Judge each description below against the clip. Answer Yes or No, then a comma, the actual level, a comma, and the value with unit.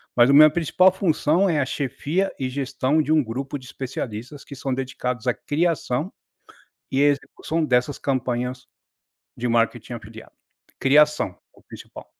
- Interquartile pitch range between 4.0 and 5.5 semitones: No, average, 3.4 semitones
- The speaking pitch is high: No, low, 135 Hz